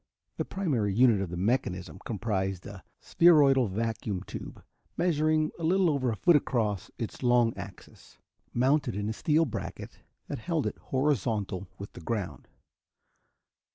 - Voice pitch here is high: No, low, 115 Hz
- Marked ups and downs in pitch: Yes, wide, 6.6 semitones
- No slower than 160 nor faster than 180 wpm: No, average, 145 wpm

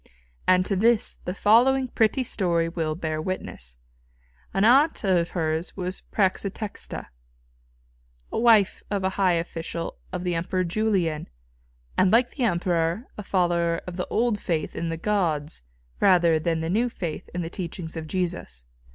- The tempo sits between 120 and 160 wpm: Yes, average, 150 wpm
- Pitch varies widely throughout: No, average, 3.7 semitones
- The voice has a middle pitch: Yes, medium, 180 Hz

